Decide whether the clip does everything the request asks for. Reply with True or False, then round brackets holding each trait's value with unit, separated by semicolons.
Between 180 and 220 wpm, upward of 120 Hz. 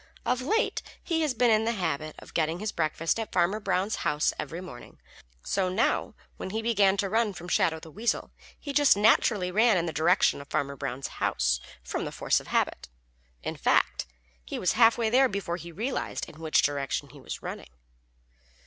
True (190 wpm; 190 Hz)